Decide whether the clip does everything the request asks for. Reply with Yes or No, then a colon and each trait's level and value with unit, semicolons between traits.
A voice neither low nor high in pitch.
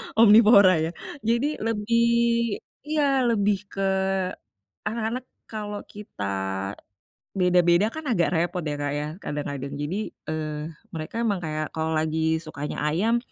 Yes: medium, 180 Hz